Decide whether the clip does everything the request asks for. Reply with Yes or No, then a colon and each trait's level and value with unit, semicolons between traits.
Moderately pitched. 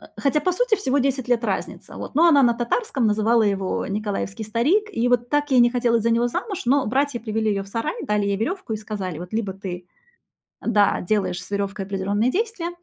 No: high, 230 Hz